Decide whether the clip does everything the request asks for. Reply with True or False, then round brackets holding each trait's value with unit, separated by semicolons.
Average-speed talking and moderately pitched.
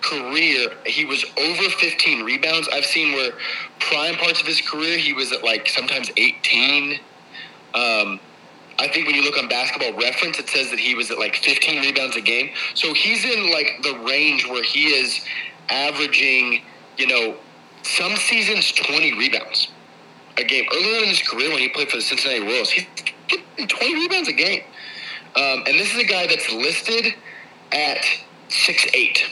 True (175 wpm; 150 Hz)